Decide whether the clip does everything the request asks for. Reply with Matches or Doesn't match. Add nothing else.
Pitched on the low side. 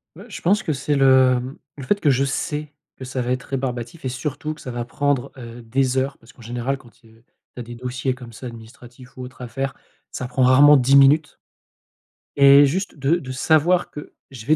Matches